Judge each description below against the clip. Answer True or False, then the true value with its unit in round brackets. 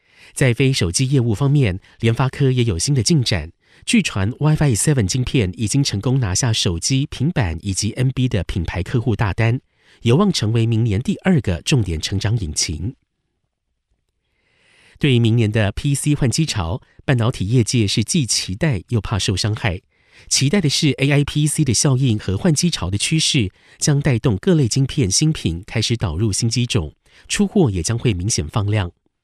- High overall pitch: False (120 Hz)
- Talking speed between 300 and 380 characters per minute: False (275 characters per minute)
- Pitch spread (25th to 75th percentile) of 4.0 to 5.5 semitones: True (5.1 semitones)